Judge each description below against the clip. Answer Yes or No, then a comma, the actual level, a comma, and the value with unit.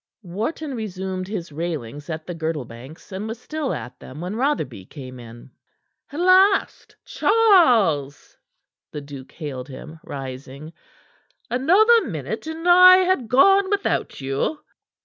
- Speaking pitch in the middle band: Yes, medium, 180 Hz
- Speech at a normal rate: No, slow, 130 wpm